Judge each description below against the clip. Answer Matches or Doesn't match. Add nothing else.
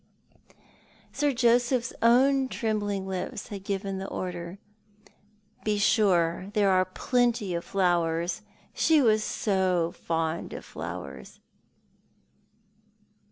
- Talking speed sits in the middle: Doesn't match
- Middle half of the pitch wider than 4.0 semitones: Matches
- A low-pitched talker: Doesn't match